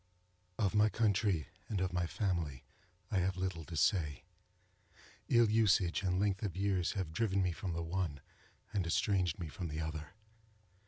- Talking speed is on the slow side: No, average, 165 wpm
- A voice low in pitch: Yes, very low, 95 Hz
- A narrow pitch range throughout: No, average, 3.2 semitones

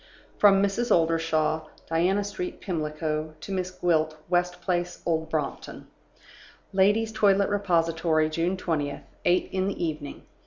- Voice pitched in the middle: Yes, medium, 175 Hz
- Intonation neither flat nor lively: Yes, average, 3.3 semitones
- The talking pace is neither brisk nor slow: No, slow, 125 wpm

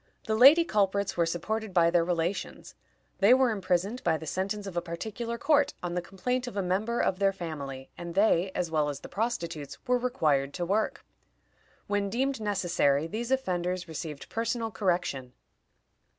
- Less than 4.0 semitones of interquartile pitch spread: No, average, 4.8 semitones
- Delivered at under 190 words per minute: Yes, average, 170 wpm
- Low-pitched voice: No, high, 190 Hz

